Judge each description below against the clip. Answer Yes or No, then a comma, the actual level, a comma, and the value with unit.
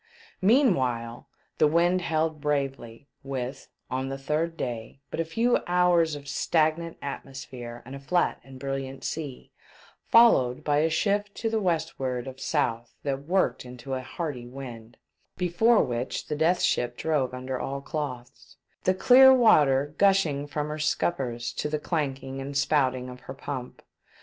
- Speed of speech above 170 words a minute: No, average, 165 wpm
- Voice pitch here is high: No, medium, 140 Hz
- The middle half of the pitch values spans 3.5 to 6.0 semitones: Yes, average, 4.3 semitones